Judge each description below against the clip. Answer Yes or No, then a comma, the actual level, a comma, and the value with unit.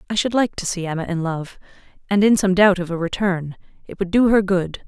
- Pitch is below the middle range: No, high, 190 Hz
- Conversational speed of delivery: No, fast, 245 wpm